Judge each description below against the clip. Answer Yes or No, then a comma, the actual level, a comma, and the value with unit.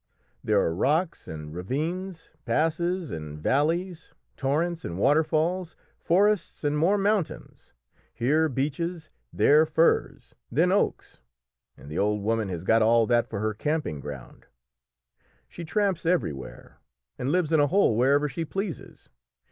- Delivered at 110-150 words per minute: Yes, slow, 135 wpm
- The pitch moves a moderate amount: No, wide, 7.3 semitones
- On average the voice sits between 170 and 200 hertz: No, medium, 150 Hz